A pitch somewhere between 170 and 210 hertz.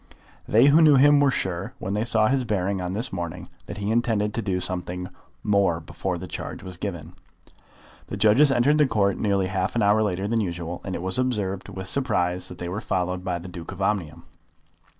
No: low, 100 Hz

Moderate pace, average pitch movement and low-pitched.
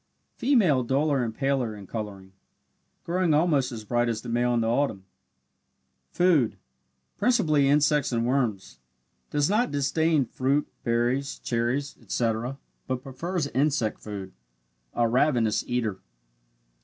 No: slow, 125 wpm; average, 4.2 semitones; low, 130 Hz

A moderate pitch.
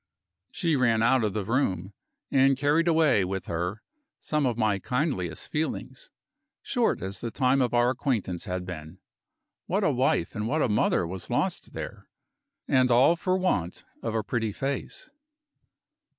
No: low, 120 Hz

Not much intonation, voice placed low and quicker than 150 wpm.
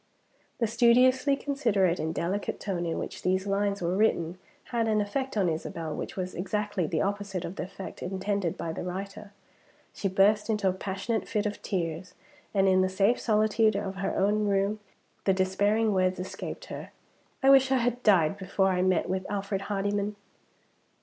No: narrow, 2.2 semitones; high, 195 Hz; average, 175 wpm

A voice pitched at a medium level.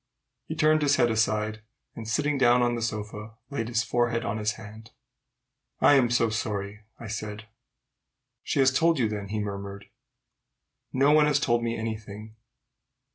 No: low, 115 Hz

